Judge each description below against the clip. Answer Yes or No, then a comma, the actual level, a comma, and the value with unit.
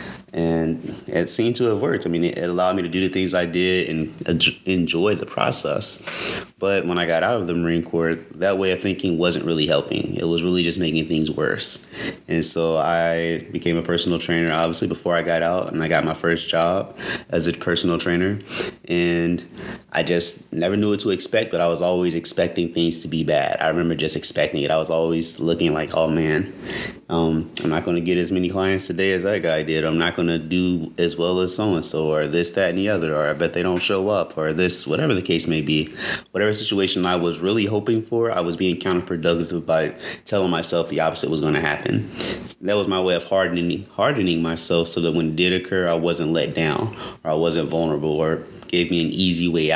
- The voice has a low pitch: Yes, very low, 85 Hz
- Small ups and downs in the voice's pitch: Yes, narrow, 1.7 semitones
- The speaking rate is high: Yes, fast, 225 wpm